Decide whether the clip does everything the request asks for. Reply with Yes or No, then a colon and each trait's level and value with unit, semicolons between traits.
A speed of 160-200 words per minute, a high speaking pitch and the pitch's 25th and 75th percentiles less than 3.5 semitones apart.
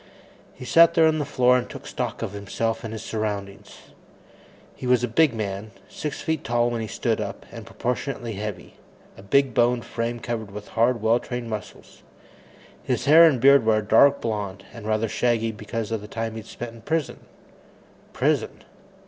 No: average, 185 wpm; low, 115 Hz; average, 2.7 semitones